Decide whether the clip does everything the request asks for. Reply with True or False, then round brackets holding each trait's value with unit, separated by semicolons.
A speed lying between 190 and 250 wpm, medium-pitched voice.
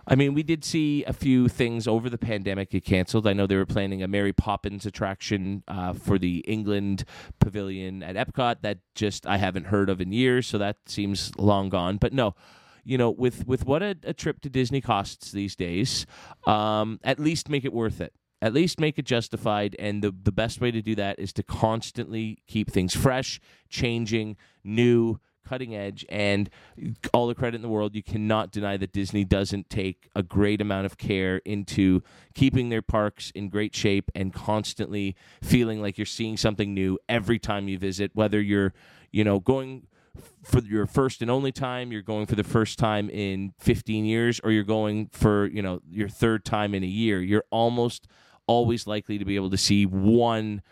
False (200 wpm; 105 Hz)